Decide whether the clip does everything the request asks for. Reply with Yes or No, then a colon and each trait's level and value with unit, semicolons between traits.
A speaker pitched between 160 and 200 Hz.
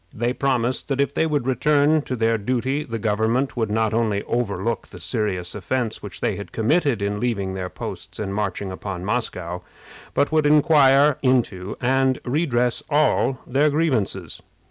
No: low, 120 Hz